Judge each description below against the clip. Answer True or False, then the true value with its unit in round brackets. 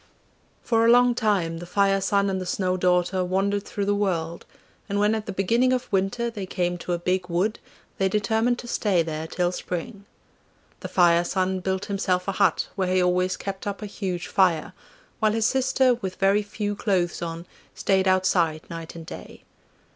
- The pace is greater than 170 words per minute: True (190 wpm)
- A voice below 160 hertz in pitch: False (190 Hz)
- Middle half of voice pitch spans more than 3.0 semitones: False (2.5 semitones)